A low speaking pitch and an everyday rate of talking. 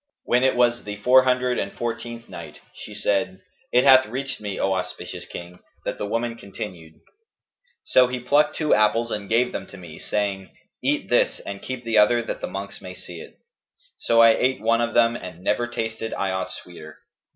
Yes: low, 115 Hz; average, 195 wpm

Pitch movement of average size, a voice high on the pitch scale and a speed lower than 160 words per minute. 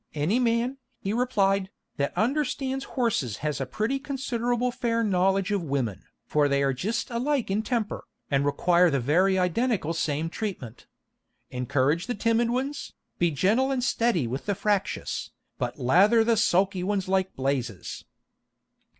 No: wide, 8.1 semitones; high, 195 Hz; average, 150 wpm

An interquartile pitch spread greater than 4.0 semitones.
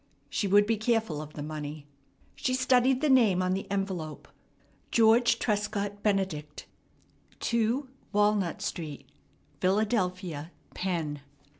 Yes: average, 5.1 semitones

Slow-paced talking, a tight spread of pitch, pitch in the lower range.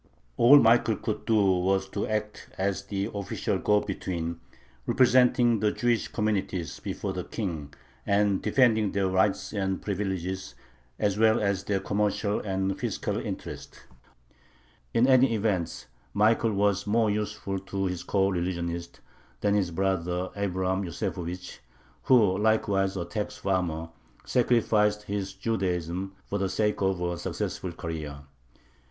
Yes: slow, 130 wpm; narrow, 2.3 semitones; low, 100 Hz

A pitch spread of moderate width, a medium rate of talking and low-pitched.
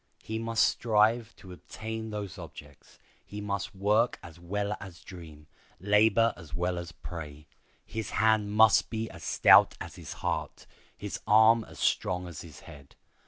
Yes: average, 4.0 semitones; average, 160 wpm; low, 105 Hz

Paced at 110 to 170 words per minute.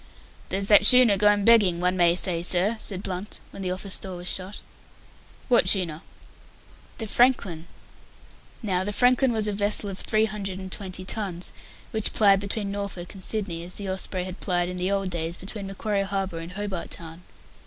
No: average, 185 wpm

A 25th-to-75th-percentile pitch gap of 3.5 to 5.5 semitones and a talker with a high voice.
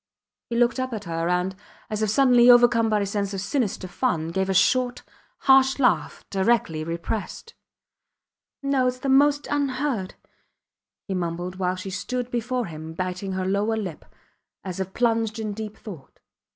Yes: average, 5.1 semitones; high, 215 Hz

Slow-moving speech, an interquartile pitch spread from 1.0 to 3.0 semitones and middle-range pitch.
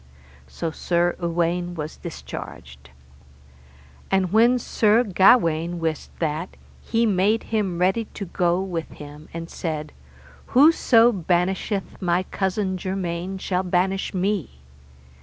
Yes: slow, 115 wpm; average, 2.7 semitones; medium, 180 Hz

